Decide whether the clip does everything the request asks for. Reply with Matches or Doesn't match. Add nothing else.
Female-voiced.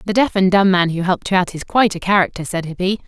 Matches